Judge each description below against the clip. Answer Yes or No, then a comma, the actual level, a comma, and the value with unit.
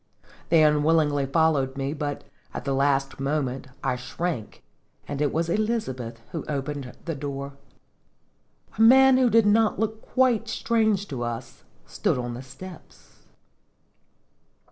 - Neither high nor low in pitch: Yes, medium, 150 Hz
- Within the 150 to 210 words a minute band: No, slow, 135 wpm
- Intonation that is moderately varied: No, wide, 7.3 semitones